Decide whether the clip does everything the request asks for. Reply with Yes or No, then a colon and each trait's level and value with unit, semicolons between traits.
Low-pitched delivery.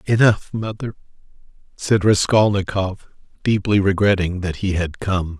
Yes: low, 100 Hz